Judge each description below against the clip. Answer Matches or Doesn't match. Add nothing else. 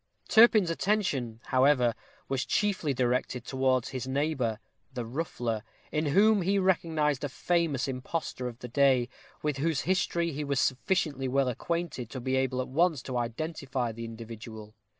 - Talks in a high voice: Doesn't match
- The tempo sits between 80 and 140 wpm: Doesn't match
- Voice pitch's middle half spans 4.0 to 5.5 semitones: Matches